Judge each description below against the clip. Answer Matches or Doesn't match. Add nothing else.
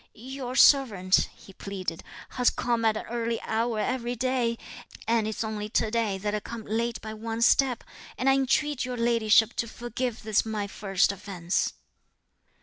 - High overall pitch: Matches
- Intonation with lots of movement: Doesn't match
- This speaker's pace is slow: Doesn't match